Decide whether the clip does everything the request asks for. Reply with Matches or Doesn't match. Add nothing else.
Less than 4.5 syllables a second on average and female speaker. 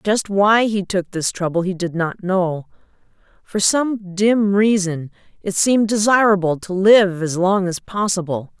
Matches